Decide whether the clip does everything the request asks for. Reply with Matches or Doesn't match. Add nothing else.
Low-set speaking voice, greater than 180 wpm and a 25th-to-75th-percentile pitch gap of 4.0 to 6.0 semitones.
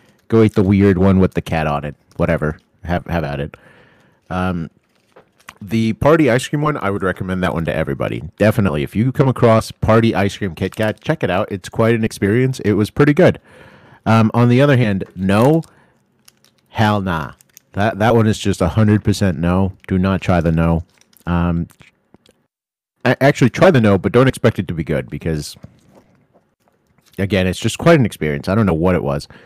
Matches